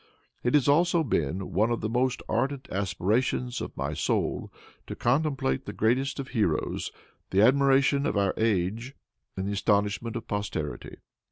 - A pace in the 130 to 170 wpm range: Yes, average, 155 wpm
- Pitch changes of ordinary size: Yes, average, 5.0 semitones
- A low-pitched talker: Yes, low, 115 Hz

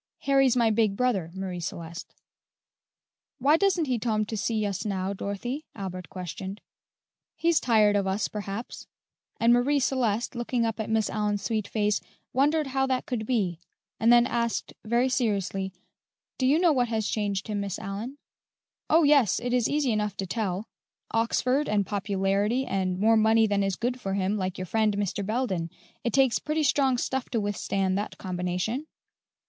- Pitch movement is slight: No, average, 4.1 semitones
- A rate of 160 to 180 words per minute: Yes, average, 170 wpm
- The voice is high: Yes, high, 220 Hz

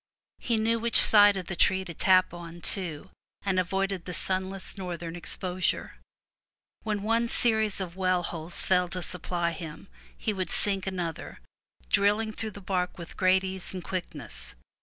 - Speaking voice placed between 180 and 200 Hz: Yes, medium, 185 Hz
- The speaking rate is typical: Yes, average, 160 wpm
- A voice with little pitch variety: Yes, narrow, 2.2 semitones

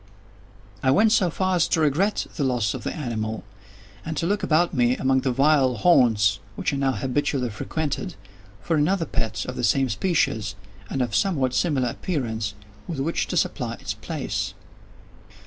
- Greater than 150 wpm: Yes, average, 170 wpm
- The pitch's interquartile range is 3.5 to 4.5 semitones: No, average, 5.2 semitones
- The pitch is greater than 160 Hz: No, low, 135 Hz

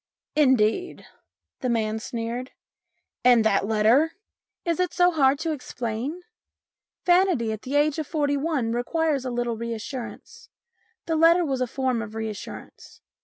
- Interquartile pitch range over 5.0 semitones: Yes, wide, 5.5 semitones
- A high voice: Yes, very high, 260 Hz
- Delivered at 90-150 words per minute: Yes, average, 145 wpm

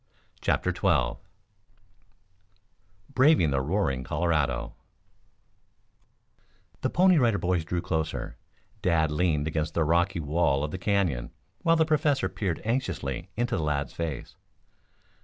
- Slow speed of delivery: Yes, slow, 115 wpm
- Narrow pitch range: No, wide, 5.4 semitones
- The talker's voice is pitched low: Yes, very low, 85 Hz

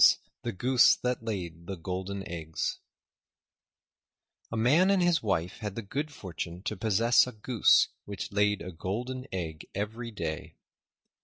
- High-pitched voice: No, low, 105 Hz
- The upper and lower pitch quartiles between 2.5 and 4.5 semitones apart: No, average, 4.9 semitones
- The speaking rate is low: No, average, 145 wpm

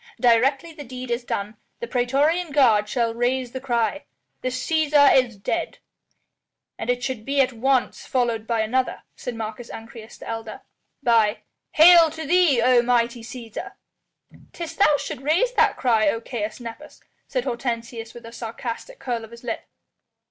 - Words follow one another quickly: No, average, 160 wpm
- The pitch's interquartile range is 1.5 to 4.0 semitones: Yes, average, 3.3 semitones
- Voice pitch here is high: Yes, high, 245 Hz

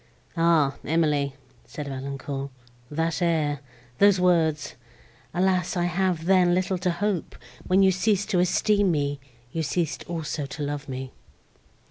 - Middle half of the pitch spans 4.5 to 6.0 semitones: No, average, 4.0 semitones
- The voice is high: No, medium, 165 Hz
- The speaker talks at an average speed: No, slow, 125 wpm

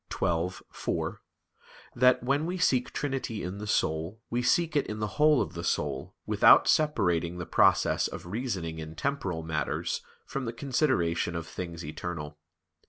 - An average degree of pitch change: No, wide, 7.9 semitones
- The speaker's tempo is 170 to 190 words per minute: No, average, 160 wpm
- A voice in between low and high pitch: No, very low, 95 Hz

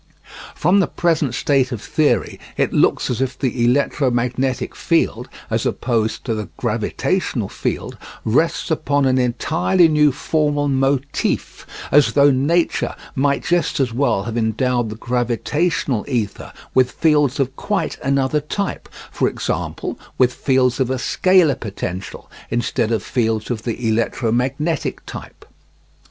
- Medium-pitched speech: No, low, 130 Hz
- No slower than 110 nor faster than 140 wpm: Yes, slow, 135 wpm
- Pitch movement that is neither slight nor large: Yes, average, 3.6 semitones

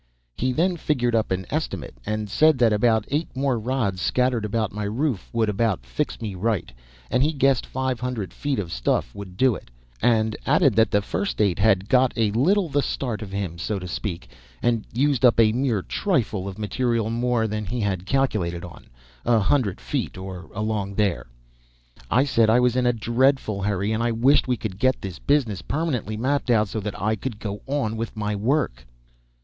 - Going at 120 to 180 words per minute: No, average, 200 wpm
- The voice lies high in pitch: No, low, 110 Hz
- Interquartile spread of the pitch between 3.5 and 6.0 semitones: Yes, average, 4.1 semitones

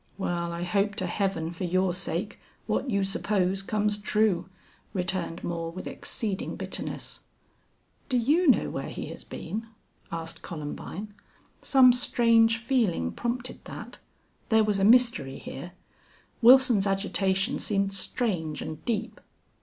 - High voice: Yes, high, 195 Hz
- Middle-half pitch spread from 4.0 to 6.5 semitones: Yes, average, 4.4 semitones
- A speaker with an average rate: No, slow, 130 wpm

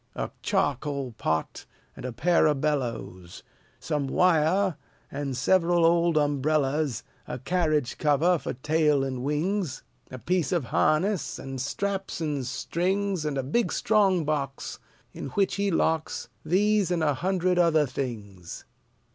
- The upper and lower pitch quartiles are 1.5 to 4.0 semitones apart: No, average, 4.8 semitones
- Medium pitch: Yes, medium, 155 Hz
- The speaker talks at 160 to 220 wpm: No, average, 140 wpm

